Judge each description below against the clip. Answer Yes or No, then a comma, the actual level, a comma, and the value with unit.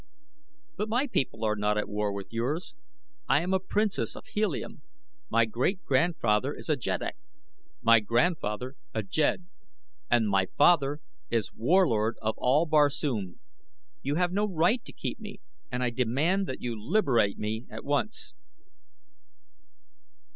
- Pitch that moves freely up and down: Yes, wide, 7.9 semitones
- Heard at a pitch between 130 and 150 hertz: Yes, low, 135 Hz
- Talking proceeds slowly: No, average, 145 wpm